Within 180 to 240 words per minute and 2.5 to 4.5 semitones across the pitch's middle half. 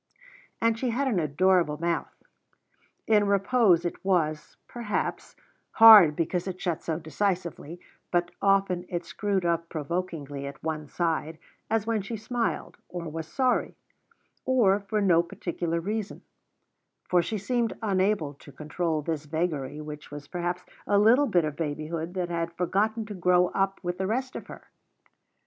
No: average, 155 wpm; average, 4.1 semitones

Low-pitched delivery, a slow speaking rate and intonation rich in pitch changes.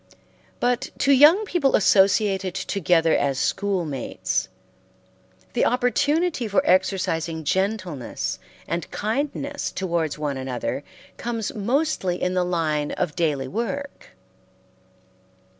No: high, 190 Hz; slow, 100 wpm; wide, 7.3 semitones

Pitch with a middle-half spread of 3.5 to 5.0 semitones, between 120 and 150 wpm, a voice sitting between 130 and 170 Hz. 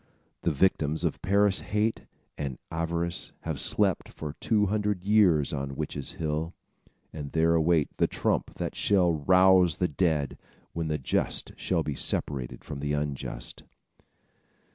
No: average, 4.1 semitones; average, 140 wpm; very low, 80 Hz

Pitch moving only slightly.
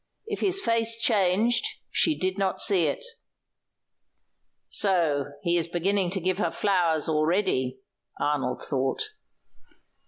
No: average, 4.8 semitones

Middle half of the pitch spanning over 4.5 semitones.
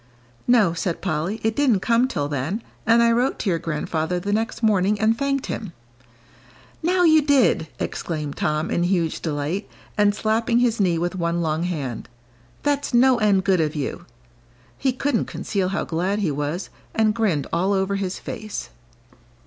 Yes: wide, 5.5 semitones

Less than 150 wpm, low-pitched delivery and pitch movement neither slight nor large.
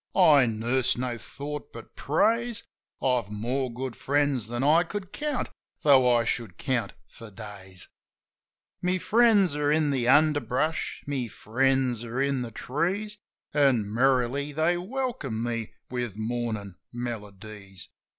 Yes: slow, 135 wpm; low, 130 Hz; average, 4.4 semitones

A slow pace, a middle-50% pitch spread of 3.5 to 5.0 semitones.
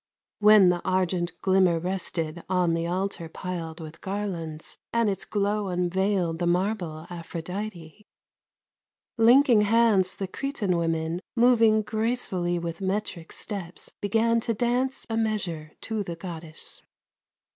Yes: slow, 125 wpm; average, 4.0 semitones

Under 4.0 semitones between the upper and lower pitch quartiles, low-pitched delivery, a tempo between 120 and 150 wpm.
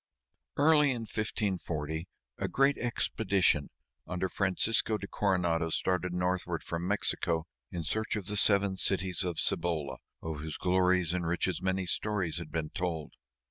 Yes: average, 3.3 semitones; very low, 90 Hz; average, 140 wpm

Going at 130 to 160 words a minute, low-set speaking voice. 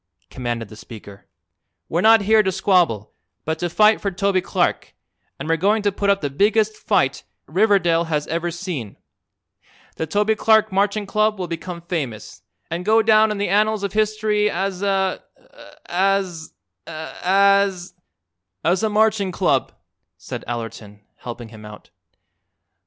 No: average, 150 wpm; high, 190 Hz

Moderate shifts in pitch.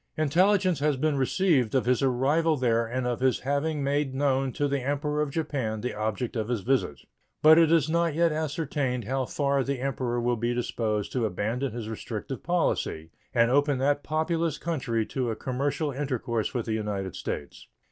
Yes: average, 3.8 semitones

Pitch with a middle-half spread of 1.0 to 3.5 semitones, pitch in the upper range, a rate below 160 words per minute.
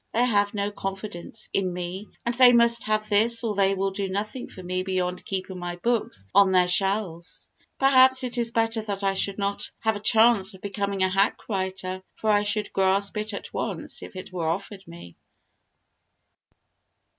No: narrow, 2.5 semitones; high, 200 Hz; average, 185 wpm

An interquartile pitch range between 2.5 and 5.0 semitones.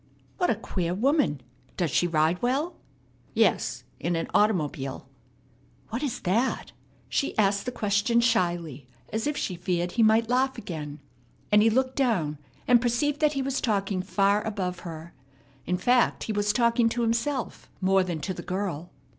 No: wide, 5.4 semitones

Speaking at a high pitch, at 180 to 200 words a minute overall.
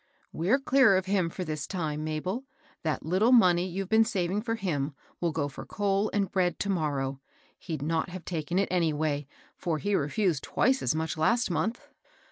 No: medium, 180 Hz; average, 195 wpm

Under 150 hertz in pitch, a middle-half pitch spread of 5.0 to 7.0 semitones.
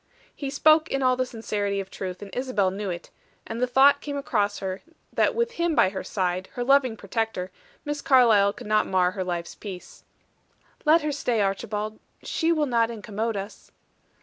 No: high, 225 Hz; wide, 5.6 semitones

